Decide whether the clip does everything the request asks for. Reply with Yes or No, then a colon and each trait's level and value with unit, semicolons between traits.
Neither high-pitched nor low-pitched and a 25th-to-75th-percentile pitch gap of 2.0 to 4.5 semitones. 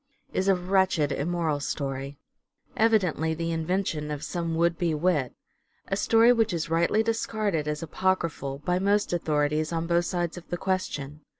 Yes: medium, 170 Hz; average, 3.6 semitones